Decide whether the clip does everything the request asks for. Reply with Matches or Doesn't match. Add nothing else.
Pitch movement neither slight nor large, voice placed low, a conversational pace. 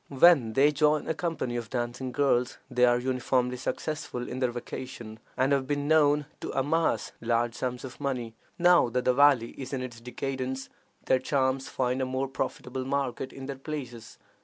Doesn't match